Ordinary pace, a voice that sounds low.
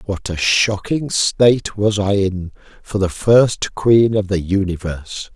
Yes: average, 155 wpm; low, 100 Hz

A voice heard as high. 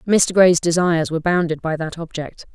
No: medium, 170 Hz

